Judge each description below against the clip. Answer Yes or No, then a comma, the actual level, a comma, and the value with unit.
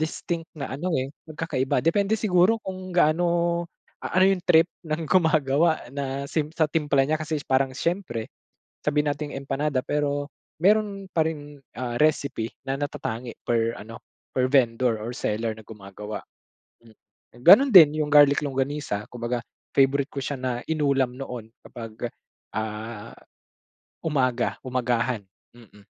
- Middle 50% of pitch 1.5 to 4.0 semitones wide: No, average, 4.8 semitones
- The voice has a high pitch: No, medium, 140 Hz